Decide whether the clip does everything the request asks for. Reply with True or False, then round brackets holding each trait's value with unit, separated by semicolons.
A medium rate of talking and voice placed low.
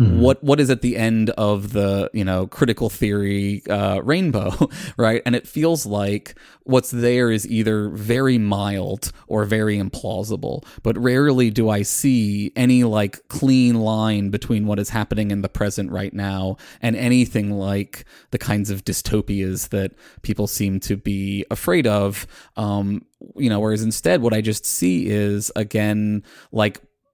True (160 wpm; 105 Hz)